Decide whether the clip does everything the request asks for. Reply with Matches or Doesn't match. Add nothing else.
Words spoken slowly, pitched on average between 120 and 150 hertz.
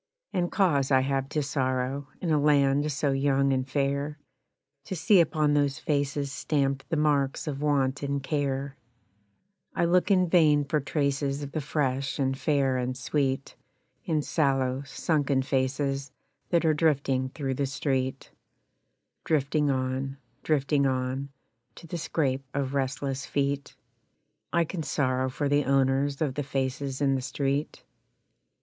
Doesn't match